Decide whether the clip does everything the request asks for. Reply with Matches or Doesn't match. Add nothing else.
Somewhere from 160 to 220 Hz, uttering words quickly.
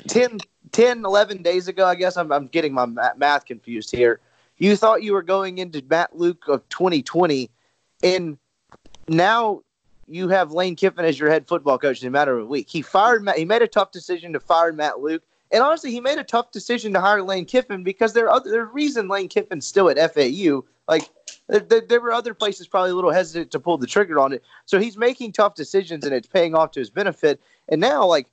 Matches